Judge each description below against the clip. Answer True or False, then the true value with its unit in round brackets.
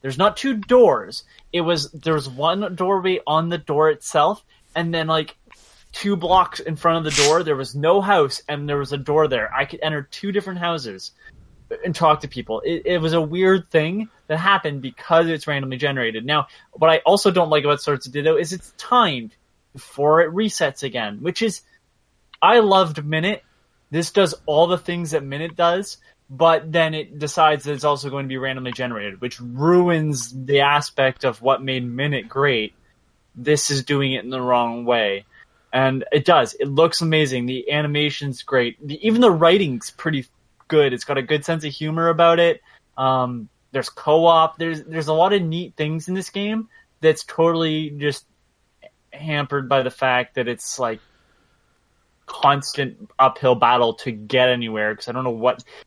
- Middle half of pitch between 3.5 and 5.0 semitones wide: True (4.1 semitones)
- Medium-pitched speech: True (155 Hz)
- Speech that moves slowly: False (185 wpm)